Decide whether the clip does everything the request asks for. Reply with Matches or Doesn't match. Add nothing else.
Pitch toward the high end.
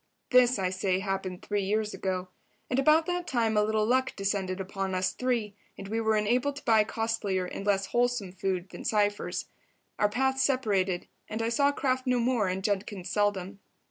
Matches